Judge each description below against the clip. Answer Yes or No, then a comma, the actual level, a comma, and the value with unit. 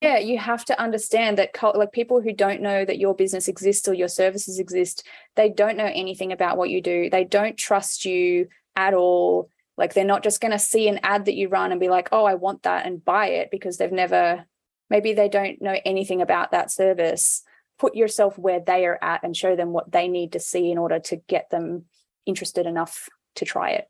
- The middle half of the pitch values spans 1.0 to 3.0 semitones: Yes, narrow, 2.5 semitones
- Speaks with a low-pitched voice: No, high, 195 Hz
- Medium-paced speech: No, fast, 230 wpm